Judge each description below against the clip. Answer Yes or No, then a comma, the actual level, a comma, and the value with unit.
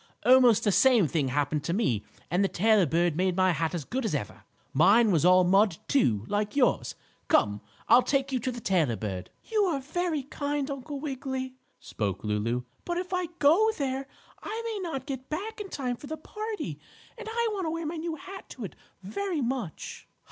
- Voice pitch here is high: Yes, very high, 260 Hz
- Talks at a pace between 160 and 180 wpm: No, average, 200 wpm